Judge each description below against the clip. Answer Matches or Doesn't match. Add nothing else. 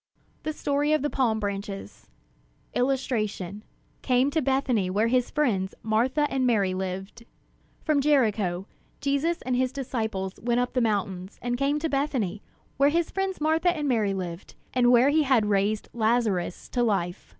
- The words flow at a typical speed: Matches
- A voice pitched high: Matches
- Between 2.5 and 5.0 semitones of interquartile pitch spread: Doesn't match